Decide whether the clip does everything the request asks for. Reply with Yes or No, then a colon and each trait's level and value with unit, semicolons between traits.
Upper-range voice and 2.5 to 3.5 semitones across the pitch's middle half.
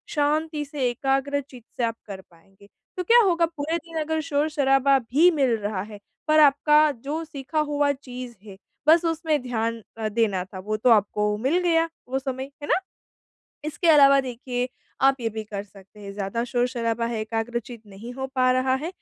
No: very high, 255 Hz; average, 5.0 semitones